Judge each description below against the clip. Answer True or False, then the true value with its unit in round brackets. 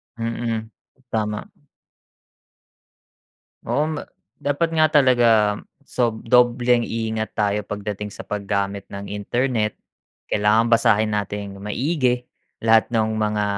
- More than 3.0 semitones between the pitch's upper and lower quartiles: False (2.7 semitones)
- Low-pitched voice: True (110 Hz)